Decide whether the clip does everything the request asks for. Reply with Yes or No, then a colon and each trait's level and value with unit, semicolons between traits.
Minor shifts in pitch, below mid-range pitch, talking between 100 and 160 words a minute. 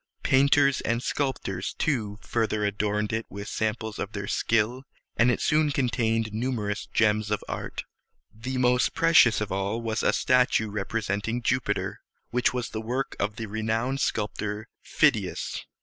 No: average, 3.0 semitones; low, 110 Hz; average, 150 wpm